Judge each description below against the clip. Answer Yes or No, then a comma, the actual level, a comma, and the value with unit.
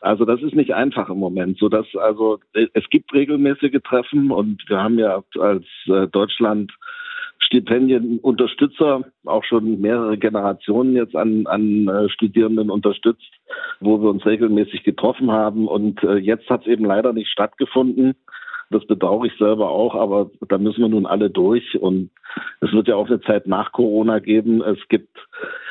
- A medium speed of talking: Yes, average, 160 wpm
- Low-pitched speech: Yes, low, 110 Hz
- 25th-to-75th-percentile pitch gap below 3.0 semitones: No, average, 3.7 semitones